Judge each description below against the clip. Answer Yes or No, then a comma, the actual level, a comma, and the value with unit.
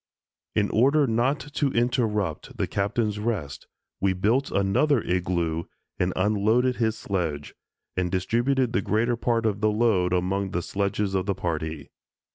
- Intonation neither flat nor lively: Yes, average, 4.4 semitones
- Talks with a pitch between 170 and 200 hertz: No, low, 105 Hz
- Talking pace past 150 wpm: No, average, 145 wpm